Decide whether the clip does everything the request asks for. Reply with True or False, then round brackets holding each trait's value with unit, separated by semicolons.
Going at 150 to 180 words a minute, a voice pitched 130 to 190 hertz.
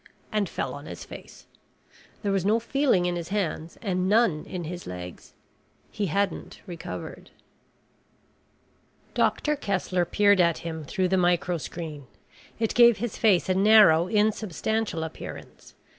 False (135 wpm; 185 Hz)